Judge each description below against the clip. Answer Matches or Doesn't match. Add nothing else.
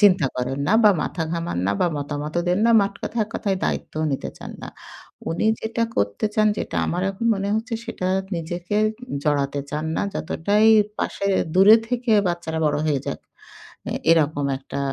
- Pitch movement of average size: Doesn't match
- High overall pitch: Doesn't match